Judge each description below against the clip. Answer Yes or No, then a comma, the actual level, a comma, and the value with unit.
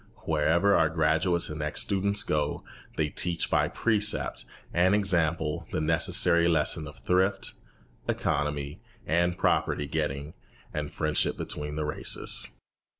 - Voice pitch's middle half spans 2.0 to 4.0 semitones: Yes, average, 2.9 semitones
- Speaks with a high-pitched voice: No, very low, 80 Hz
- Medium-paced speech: No, slow, 125 wpm